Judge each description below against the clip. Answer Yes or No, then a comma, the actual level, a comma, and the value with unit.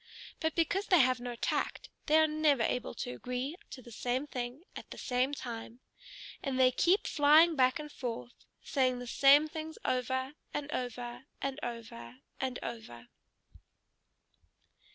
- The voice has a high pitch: Yes, very high, 255 Hz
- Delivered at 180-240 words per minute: No, average, 155 wpm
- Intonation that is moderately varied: Yes, average, 3.5 semitones